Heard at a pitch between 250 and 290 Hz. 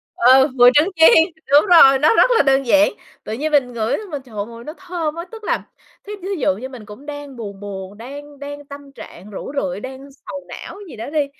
Yes: very high, 270 Hz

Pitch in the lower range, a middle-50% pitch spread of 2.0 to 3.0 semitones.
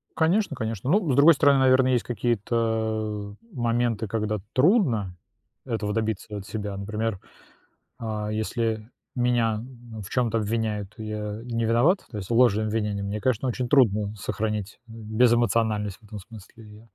Yes: low, 110 Hz; narrow, 2.4 semitones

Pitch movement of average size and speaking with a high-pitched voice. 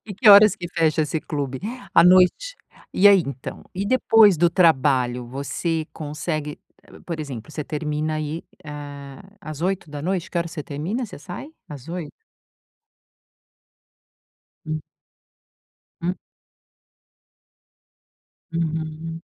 No: average, 3.5 semitones; medium, 160 Hz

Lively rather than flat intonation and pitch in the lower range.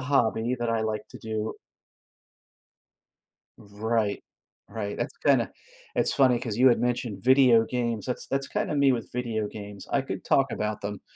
No: average, 2.9 semitones; low, 115 Hz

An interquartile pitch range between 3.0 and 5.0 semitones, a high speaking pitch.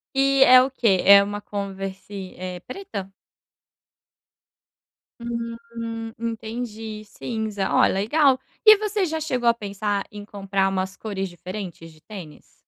Yes: average, 3.3 semitones; high, 215 Hz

